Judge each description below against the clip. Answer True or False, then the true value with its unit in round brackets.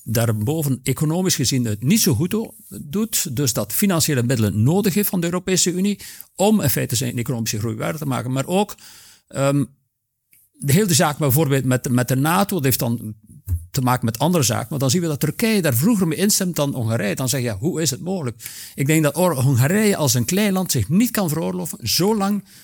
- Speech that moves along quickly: True (210 wpm)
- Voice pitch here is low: False (145 Hz)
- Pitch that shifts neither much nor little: False (6.7 semitones)